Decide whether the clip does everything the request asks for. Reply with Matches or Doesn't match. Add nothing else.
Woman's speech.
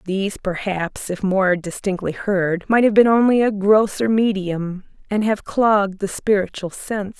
Matches